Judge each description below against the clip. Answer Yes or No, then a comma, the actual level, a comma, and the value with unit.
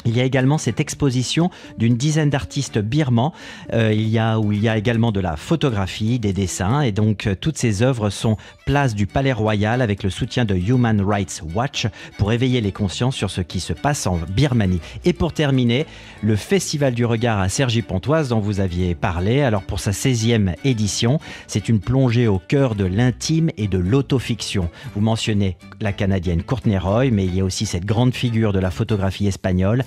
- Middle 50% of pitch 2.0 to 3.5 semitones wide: No, average, 4.8 semitones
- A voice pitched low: Yes, low, 115 Hz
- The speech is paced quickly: No, average, 200 wpm